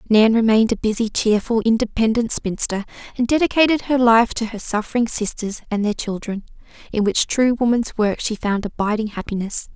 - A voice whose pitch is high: Yes, high, 225 Hz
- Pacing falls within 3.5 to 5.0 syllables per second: No, 5.5 syllables/s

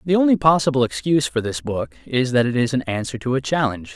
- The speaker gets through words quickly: Yes, fast, 245 wpm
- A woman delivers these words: No, male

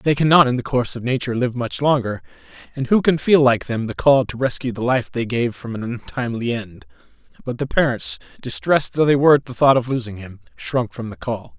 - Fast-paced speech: Yes, fast, 235 wpm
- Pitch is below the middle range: Yes, low, 125 Hz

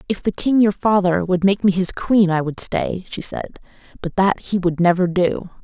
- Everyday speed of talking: No, fast, 225 wpm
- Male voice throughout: No, female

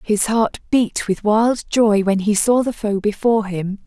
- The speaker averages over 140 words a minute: Yes, average, 200 wpm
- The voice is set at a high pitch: Yes, high, 215 Hz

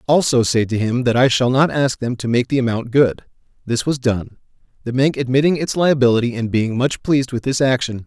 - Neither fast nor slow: No, fast, 225 wpm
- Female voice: No, male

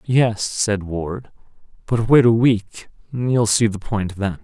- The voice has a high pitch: No, low, 110 Hz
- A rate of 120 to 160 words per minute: Yes, average, 150 wpm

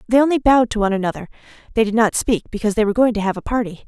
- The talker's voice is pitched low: No, high, 220 Hz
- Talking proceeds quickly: Yes, fast, 280 wpm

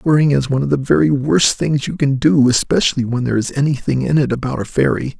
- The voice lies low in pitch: Yes, low, 130 Hz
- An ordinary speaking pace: No, fast, 245 wpm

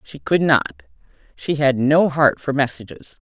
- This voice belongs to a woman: Yes, female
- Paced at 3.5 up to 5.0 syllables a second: Yes, 4.3 syllables/s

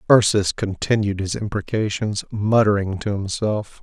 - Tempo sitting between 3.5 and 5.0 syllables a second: Yes, 4.5 syllables/s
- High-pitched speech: No, low, 105 Hz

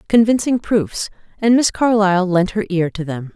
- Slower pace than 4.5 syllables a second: No, 4.9 syllables/s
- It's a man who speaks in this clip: No, female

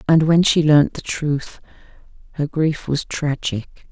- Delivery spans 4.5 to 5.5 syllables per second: No, 3.7 syllables/s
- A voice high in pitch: No, medium, 150 Hz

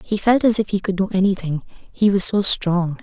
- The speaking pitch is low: No, high, 195 Hz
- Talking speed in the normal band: No, fast, 240 wpm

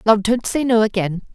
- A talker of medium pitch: No, high, 220 Hz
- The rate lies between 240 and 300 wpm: No, fast, 225 wpm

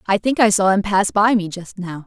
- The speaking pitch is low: No, high, 195 Hz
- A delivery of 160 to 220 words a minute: No, fast, 290 wpm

